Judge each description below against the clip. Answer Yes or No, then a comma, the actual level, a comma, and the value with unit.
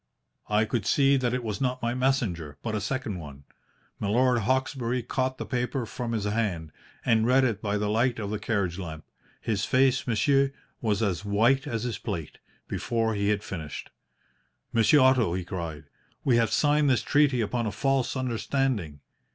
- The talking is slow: No, average, 175 wpm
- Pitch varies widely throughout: No, average, 4.2 semitones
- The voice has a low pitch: Yes, low, 115 Hz